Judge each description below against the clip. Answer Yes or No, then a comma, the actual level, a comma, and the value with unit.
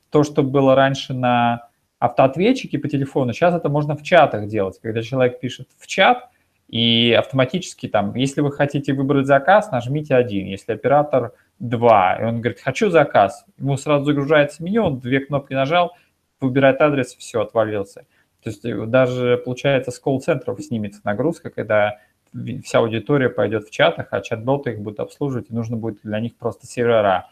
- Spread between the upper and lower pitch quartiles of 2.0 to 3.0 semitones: No, average, 3.7 semitones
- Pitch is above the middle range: No, low, 135 Hz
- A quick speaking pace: Yes, fast, 165 wpm